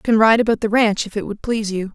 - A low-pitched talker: No, high, 215 Hz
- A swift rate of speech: Yes, fast, 340 wpm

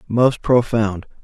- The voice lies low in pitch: Yes, low, 115 Hz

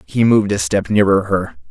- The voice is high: No, low, 100 Hz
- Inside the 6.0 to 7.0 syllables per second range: No, 5.3 syllables/s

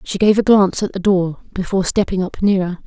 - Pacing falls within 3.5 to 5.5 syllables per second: No, 6.0 syllables/s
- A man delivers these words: No, female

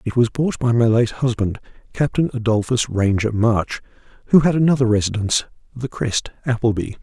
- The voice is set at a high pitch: No, low, 120 Hz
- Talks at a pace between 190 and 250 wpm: No, average, 155 wpm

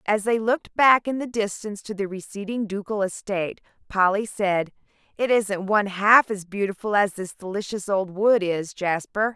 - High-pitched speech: Yes, high, 205 Hz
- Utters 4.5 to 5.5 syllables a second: Yes, 4.9 syllables/s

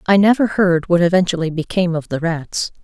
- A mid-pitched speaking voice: Yes, medium, 175 Hz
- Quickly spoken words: No, average, 190 wpm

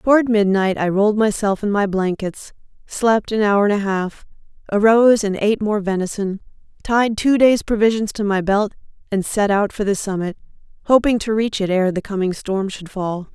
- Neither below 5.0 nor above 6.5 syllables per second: Yes, 5.1 syllables/s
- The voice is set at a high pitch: Yes, high, 205 Hz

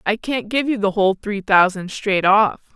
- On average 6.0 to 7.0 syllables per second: No, 4.8 syllables/s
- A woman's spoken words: Yes, female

